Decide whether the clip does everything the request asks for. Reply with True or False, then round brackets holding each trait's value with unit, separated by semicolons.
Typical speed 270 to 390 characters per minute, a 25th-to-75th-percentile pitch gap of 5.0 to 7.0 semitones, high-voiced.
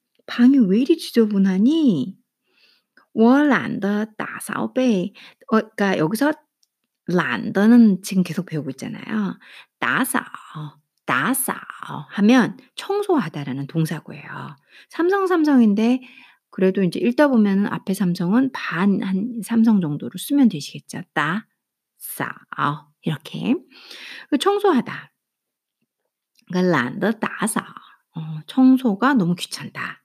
False (230 characters per minute; 5.5 semitones; 220 Hz)